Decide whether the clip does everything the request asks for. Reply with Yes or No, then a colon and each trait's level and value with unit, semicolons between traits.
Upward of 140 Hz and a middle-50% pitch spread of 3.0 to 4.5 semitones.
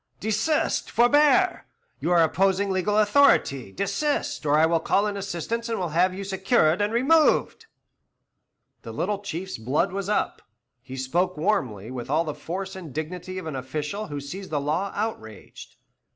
No: medium, 185 Hz; average, 5.2 semitones